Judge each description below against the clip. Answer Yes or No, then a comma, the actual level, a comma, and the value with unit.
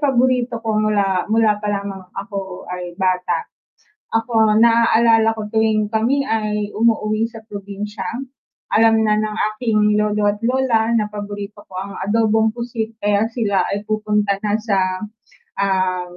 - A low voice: No, high, 215 Hz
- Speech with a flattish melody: Yes, narrow, 1.7 semitones